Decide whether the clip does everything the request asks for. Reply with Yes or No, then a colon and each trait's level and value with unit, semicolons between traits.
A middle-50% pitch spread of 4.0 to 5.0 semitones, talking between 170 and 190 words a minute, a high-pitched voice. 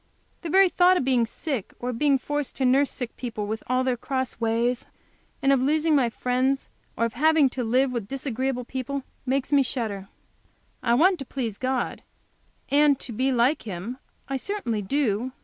No: average, 2.9 semitones; average, 185 wpm; very high, 260 Hz